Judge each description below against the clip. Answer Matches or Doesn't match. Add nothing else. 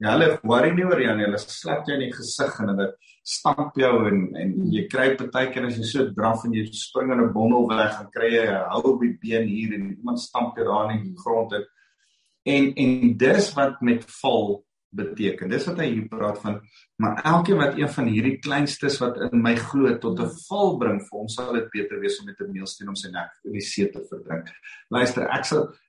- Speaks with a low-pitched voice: Matches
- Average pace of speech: Doesn't match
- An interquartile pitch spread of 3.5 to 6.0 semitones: Matches